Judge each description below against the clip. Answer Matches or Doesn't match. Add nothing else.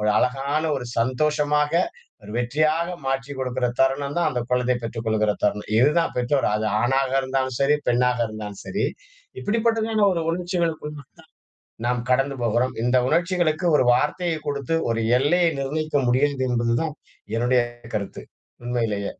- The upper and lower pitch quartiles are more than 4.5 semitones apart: Doesn't match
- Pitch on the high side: Doesn't match